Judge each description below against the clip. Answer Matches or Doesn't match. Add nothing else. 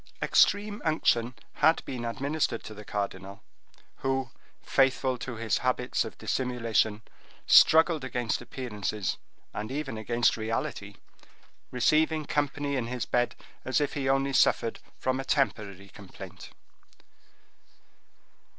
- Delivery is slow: Matches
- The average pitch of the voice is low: Matches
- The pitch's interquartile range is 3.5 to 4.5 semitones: Matches